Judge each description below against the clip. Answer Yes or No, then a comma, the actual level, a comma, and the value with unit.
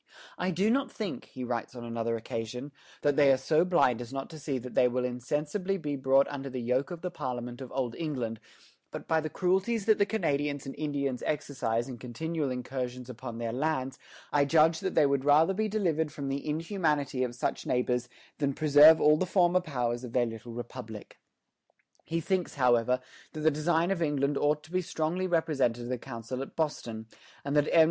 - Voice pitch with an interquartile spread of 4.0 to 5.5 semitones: Yes, average, 4.4 semitones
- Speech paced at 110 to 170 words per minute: No, average, 200 wpm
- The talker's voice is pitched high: No, medium, 140 Hz